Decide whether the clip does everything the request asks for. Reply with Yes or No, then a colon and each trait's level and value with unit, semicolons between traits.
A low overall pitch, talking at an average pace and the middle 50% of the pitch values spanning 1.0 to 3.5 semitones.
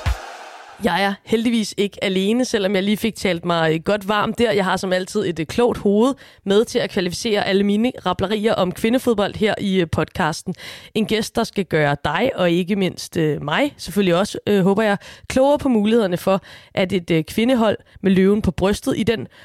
No: high, 200 Hz; average, 190 wpm; average, 3.0 semitones